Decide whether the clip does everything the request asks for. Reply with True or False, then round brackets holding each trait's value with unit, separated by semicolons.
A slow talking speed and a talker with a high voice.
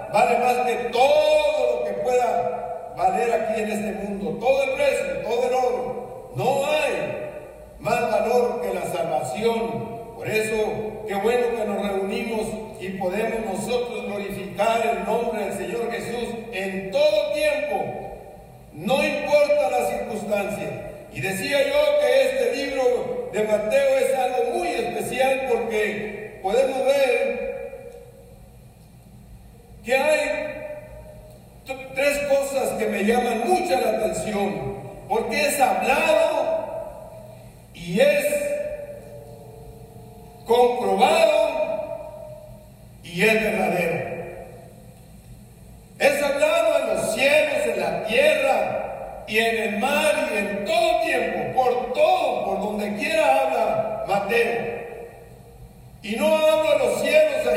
True (115 wpm; 235 Hz)